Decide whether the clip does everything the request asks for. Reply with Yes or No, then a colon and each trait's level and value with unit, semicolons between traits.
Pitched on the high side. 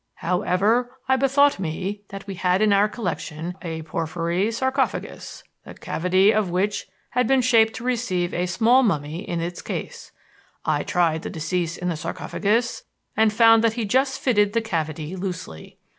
Yes: high, 195 Hz